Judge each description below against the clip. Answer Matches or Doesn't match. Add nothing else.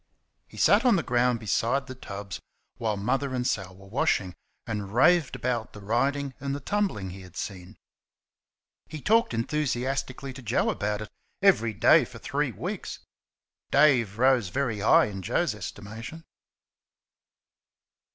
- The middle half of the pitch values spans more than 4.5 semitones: Matches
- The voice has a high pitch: Doesn't match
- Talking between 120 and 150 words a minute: Matches